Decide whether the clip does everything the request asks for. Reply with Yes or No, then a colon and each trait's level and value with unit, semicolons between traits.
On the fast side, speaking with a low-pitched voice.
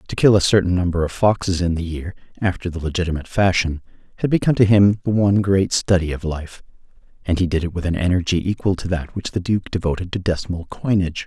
Yes: fast, 215 wpm; very low, 90 Hz